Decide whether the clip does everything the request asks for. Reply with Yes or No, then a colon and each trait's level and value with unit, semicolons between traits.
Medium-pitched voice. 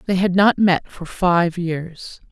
Yes: medium, 180 Hz